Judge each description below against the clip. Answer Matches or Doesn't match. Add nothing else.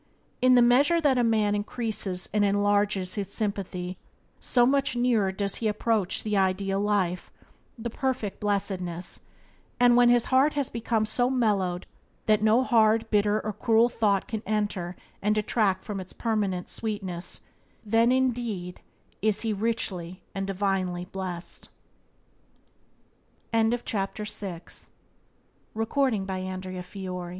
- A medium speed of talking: Doesn't match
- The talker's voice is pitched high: Matches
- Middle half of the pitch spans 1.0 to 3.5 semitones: Matches